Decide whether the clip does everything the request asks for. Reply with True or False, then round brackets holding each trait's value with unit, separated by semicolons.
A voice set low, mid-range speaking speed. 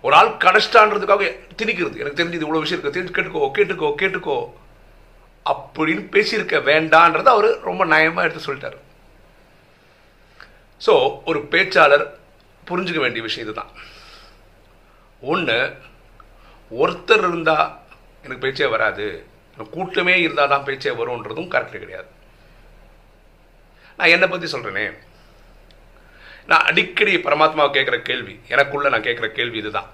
False (200 Hz; 110 wpm)